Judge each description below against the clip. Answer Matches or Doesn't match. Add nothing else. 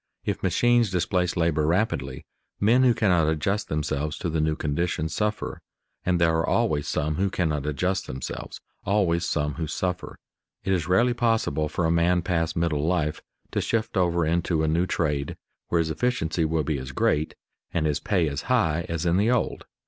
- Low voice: Matches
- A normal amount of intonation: Matches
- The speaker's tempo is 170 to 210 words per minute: Matches